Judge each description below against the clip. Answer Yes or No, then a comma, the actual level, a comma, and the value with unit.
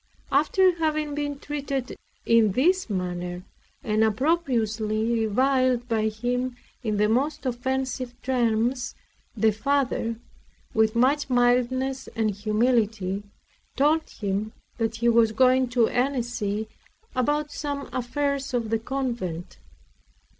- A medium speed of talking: No, slow, 110 wpm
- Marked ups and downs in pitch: No, average, 3.6 semitones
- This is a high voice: Yes, high, 245 Hz